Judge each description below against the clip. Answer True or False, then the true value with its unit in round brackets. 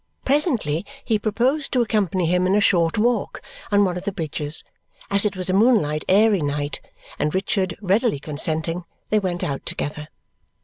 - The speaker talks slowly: False (170 wpm)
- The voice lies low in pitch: False (185 Hz)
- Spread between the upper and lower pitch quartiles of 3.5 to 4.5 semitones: False (5.0 semitones)